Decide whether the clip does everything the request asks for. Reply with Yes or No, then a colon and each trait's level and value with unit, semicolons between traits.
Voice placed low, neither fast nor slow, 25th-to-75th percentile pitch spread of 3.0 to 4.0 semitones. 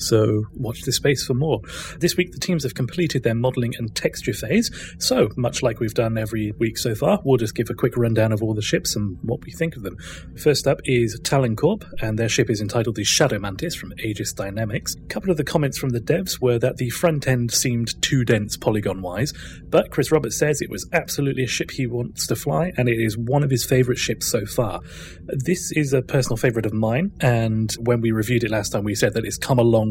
No: low, 120 Hz; fast, 240 wpm; average, 3.6 semitones